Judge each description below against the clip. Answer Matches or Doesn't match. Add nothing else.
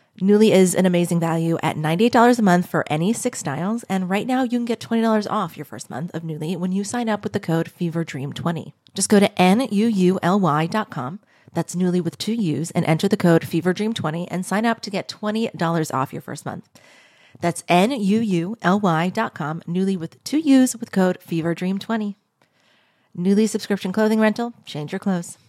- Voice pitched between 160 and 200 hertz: Matches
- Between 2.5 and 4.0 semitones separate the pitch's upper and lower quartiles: Doesn't match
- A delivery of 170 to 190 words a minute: Matches